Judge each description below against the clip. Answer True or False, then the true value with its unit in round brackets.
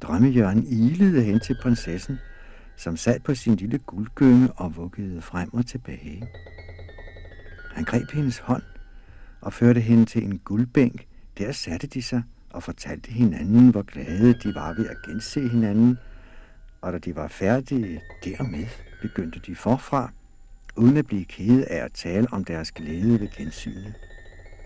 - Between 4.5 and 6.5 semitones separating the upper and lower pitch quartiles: True (5.2 semitones)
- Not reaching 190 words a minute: True (150 wpm)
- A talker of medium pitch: False (110 Hz)